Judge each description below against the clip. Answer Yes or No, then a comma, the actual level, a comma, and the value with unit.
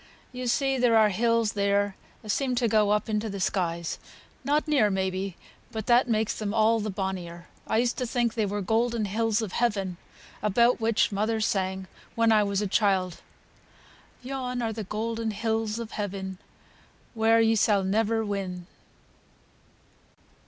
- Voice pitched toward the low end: No, high, 215 Hz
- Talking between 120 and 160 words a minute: No, average, 170 wpm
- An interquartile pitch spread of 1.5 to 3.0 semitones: Yes, narrow, 2.5 semitones